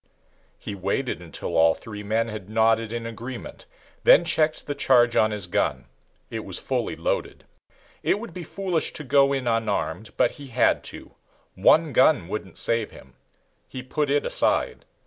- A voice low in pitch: Yes, low, 115 Hz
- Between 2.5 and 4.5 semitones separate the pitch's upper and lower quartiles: No, average, 4.9 semitones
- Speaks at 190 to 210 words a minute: No, average, 165 wpm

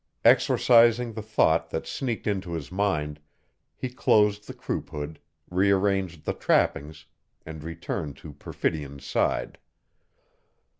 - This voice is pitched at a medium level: No, very low, 90 Hz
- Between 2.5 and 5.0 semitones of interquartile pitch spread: No, wide, 5.5 semitones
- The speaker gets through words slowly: Yes, slow, 115 wpm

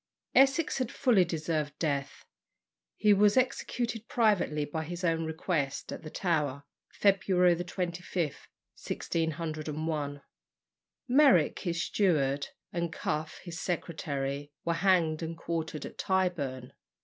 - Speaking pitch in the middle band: Yes, medium, 165 Hz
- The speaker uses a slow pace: Yes, slow, 115 wpm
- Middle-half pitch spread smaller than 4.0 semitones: Yes, average, 3.6 semitones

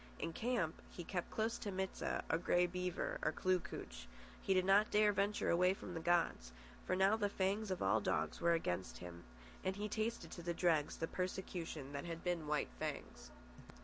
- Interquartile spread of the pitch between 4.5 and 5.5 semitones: No, average, 3.0 semitones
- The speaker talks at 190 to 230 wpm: Yes, average, 200 wpm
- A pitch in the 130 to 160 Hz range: No, medium, 180 Hz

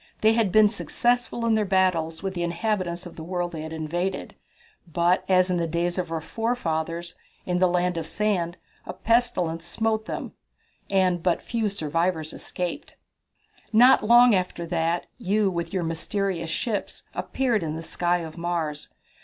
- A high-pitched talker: No, medium, 180 Hz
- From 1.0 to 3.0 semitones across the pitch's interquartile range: No, average, 3.9 semitones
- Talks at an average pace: Yes, average, 165 wpm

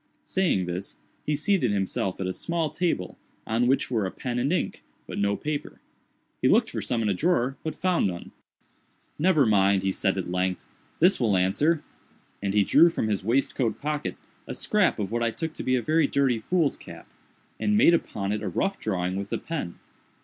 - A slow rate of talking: No, average, 195 wpm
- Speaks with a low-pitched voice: Yes, low, 120 Hz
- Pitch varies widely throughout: Yes, wide, 8.2 semitones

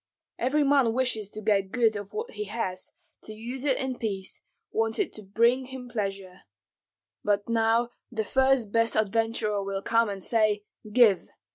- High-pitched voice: Yes, high, 225 Hz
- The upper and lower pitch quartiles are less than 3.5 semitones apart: Yes, average, 3.0 semitones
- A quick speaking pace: No, average, 165 wpm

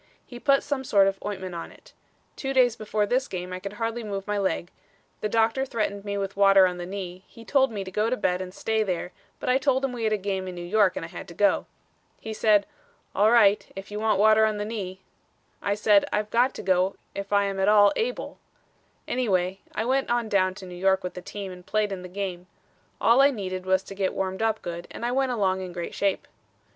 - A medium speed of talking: No, fast, 245 wpm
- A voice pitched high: Yes, high, 200 Hz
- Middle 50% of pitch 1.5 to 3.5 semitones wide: Yes, average, 3.0 semitones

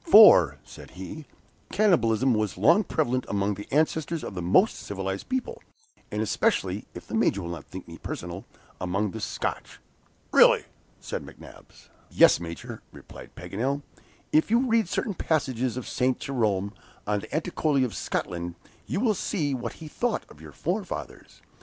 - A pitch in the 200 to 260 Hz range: No, low, 125 Hz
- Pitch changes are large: Yes, wide, 8.5 semitones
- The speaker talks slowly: No, average, 160 wpm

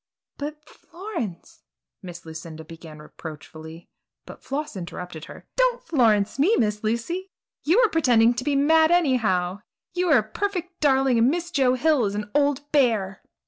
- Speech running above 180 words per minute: No, average, 155 wpm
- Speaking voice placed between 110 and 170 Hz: No, very high, 250 Hz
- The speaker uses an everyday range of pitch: No, wide, 8.4 semitones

